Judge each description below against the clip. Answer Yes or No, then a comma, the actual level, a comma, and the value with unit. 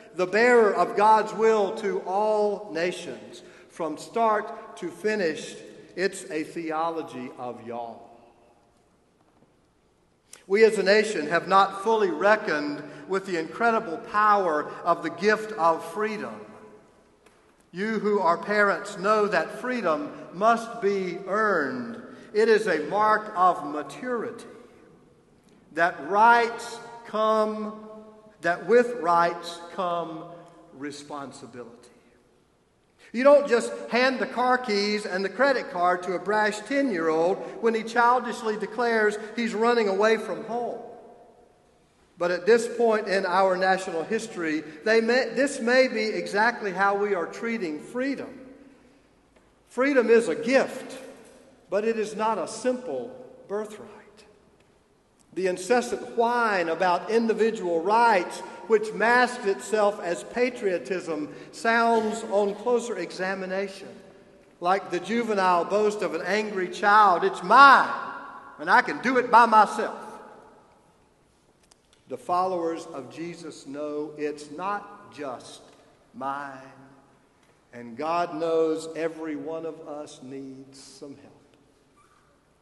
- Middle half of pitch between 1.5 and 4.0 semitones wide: No, average, 5.3 semitones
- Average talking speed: No, slow, 120 wpm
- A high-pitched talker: Yes, high, 205 Hz